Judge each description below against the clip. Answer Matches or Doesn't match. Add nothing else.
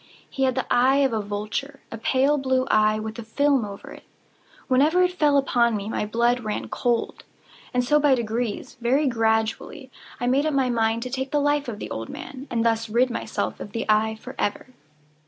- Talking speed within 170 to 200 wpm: Matches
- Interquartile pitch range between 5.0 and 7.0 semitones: Doesn't match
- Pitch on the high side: Matches